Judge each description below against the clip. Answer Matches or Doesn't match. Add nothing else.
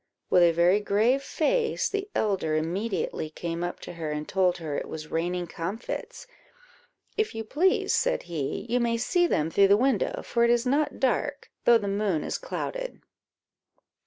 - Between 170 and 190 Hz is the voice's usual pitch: Doesn't match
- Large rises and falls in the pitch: Matches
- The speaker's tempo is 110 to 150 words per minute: Doesn't match